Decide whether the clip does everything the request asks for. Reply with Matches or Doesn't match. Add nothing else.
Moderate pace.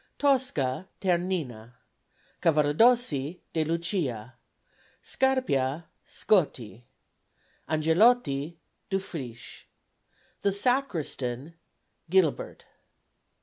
Doesn't match